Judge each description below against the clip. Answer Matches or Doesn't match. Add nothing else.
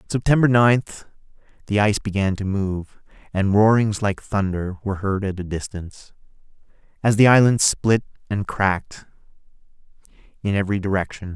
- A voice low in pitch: Matches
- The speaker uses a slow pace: Matches